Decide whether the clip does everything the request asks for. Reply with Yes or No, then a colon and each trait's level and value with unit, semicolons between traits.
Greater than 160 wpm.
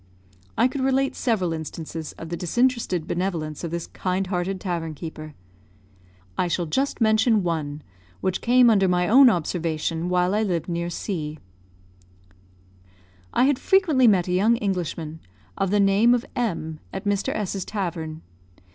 No: average, 155 wpm